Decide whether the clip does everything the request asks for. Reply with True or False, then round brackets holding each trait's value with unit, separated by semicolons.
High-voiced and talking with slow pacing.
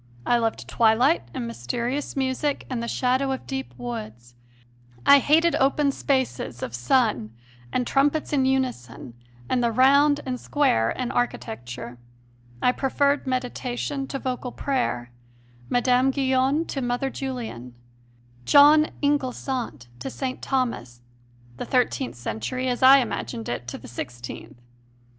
True (255 Hz; 130 wpm)